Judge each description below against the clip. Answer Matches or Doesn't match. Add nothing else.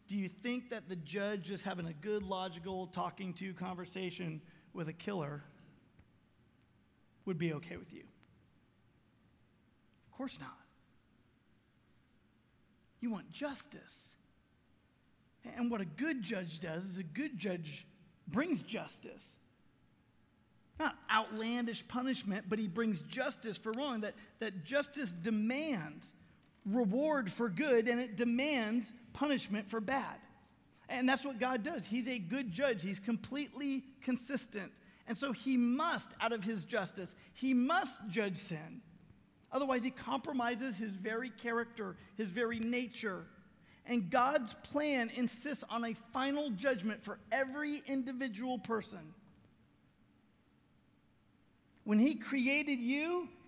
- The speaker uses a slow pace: Matches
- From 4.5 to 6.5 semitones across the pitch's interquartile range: Matches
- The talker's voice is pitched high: Matches